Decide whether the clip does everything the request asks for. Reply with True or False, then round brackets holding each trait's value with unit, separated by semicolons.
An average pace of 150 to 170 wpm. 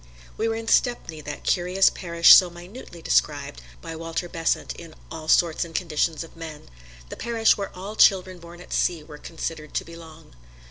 False (180 wpm)